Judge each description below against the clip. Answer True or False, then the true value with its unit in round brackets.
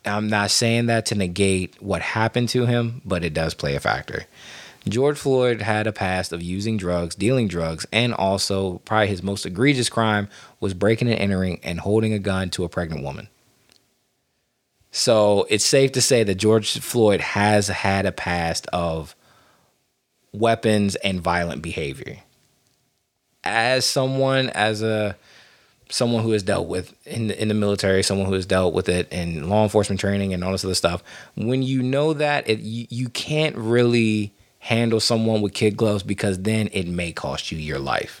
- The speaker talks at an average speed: True (175 wpm)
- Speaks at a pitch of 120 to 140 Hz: False (105 Hz)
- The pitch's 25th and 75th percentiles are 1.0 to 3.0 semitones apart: False (3.5 semitones)